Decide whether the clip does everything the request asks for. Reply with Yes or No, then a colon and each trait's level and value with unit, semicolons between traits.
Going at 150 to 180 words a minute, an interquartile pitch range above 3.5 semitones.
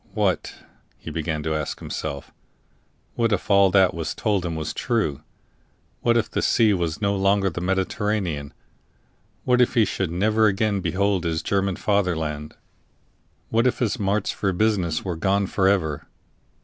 Yes: average, 160 wpm; average, 3.9 semitones